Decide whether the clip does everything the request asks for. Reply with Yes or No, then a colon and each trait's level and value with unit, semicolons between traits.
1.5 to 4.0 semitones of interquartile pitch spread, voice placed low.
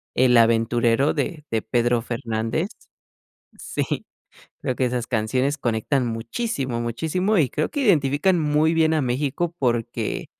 No: average, 4.8 semitones; low, 130 Hz